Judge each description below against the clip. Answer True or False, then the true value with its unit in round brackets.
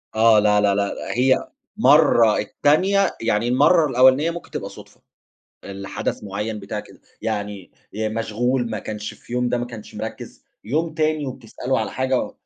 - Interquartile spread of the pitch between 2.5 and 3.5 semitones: False (4.0 semitones)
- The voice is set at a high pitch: False (120 Hz)